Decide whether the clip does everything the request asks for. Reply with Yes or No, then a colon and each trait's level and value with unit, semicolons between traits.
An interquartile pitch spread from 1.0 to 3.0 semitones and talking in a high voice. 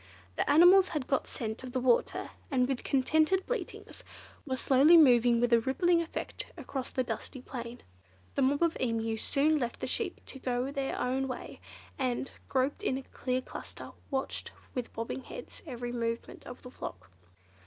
Yes: average, 2.7 semitones; very high, 260 Hz